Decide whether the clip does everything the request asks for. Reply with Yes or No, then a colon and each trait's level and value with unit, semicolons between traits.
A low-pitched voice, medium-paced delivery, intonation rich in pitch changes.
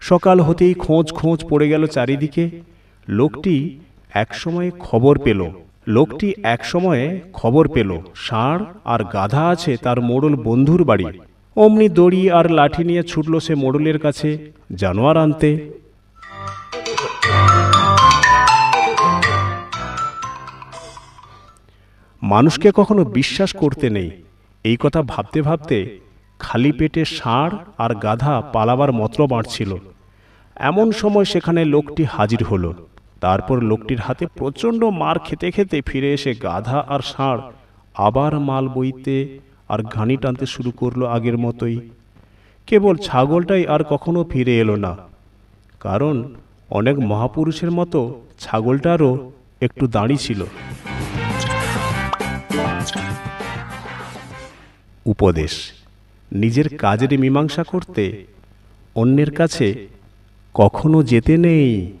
Yes: low, 130 Hz; average, 95 wpm; wide, 7.2 semitones